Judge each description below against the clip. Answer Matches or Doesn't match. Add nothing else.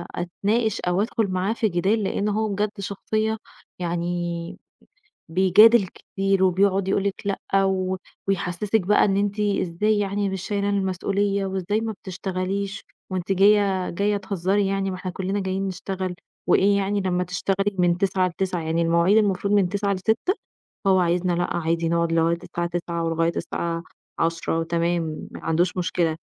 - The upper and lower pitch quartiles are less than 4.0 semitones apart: Matches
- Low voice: Doesn't match